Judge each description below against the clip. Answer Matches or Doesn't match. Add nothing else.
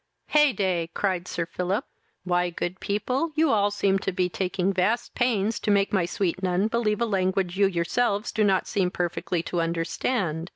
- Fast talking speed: Doesn't match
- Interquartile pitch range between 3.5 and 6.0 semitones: Doesn't match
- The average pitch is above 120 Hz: Matches